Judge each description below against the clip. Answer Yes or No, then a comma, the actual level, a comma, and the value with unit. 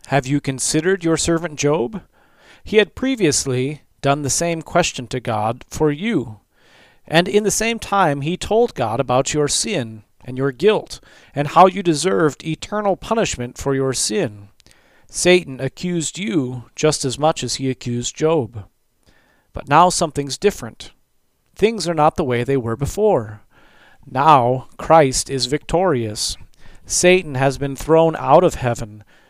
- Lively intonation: Yes, wide, 5.8 semitones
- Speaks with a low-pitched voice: No, medium, 145 Hz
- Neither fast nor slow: Yes, average, 150 wpm